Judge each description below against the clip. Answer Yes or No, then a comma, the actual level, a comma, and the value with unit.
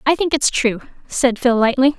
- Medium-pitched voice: No, very high, 255 Hz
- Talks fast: Yes, fast, 210 wpm